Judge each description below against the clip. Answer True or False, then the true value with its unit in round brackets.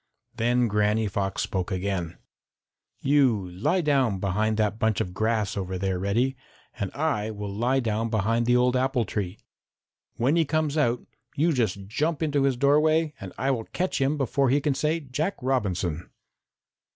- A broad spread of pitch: True (5.7 semitones)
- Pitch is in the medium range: False (120 Hz)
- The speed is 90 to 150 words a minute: False (165 wpm)